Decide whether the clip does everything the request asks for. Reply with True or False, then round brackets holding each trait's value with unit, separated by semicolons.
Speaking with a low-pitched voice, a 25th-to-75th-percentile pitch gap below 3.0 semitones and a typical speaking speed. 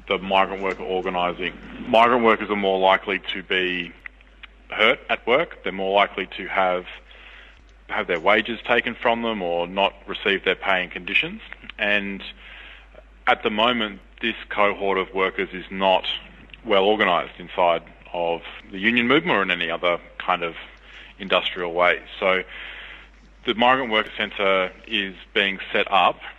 True (95 Hz; 2.5 semitones; 150 wpm)